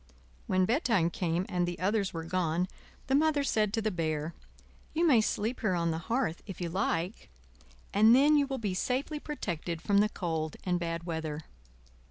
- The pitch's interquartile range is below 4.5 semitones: No, wide, 5.4 semitones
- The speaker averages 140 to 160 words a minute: No, average, 185 wpm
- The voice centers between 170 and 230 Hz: Yes, medium, 185 Hz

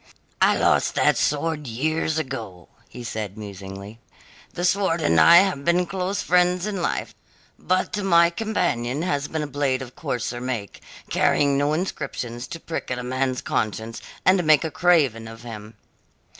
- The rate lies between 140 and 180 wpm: Yes, average, 160 wpm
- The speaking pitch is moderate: Yes, medium, 145 Hz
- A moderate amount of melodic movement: No, wide, 6.6 semitones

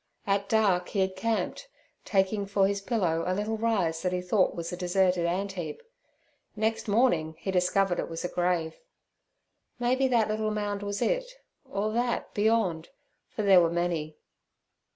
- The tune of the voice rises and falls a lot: No, average, 3.5 semitones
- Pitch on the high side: Yes, high, 195 Hz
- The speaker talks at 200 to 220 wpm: No, average, 155 wpm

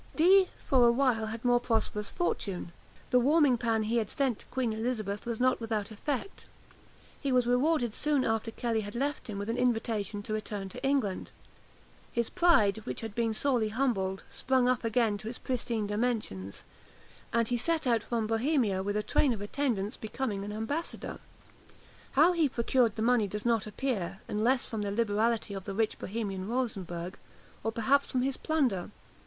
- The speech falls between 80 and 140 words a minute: No, average, 180 wpm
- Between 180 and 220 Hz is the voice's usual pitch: No, high, 230 Hz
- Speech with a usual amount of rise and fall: Yes, average, 3.3 semitones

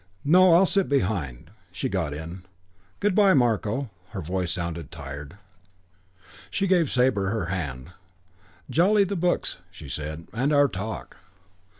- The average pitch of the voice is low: Yes, low, 100 Hz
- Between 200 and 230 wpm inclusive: No, slow, 135 wpm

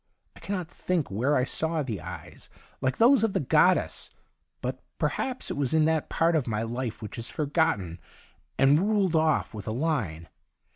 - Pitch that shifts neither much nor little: No, wide, 6.1 semitones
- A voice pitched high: No, medium, 150 Hz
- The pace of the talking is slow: No, average, 185 wpm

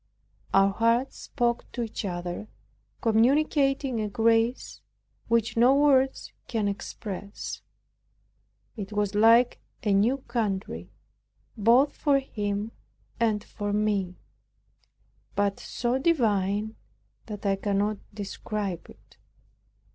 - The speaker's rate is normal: No, slow, 100 wpm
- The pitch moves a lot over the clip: No, average, 2.9 semitones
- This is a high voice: Yes, high, 220 Hz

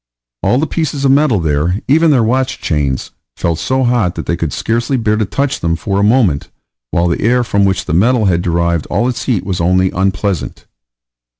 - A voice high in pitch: No, low, 100 Hz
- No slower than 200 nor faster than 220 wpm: Yes, fast, 205 wpm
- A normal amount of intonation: No, wide, 6.5 semitones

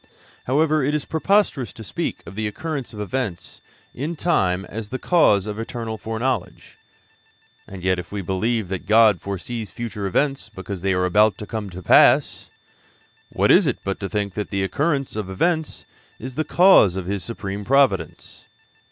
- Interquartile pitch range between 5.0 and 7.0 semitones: Yes, wide, 5.5 semitones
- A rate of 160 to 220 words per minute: Yes, average, 175 wpm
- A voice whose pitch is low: Yes, low, 110 Hz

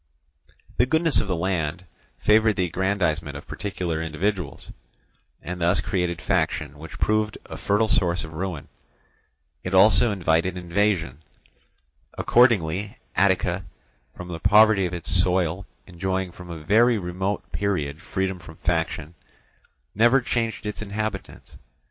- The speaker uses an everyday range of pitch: Yes, average, 3.6 semitones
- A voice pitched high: No, very low, 95 Hz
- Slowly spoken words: Yes, slow, 130 wpm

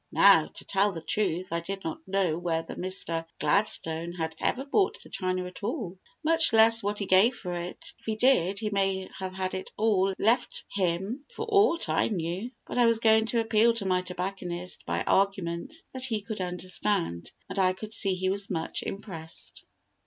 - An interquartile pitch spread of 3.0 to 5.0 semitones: Yes, average, 3.5 semitones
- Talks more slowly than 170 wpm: No, average, 190 wpm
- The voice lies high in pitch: Yes, high, 195 Hz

